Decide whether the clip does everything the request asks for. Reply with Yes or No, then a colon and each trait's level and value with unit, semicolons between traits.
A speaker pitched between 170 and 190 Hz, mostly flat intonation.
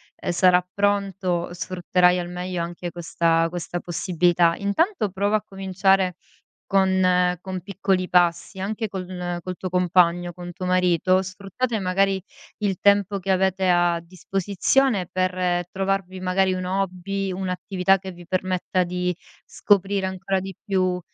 Yes: medium, 185 Hz; narrow, 1.5 semitones